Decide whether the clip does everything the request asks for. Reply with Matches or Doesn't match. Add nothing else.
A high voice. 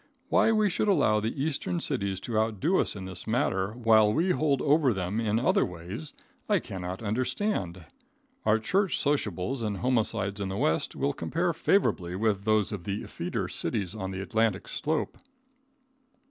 Doesn't match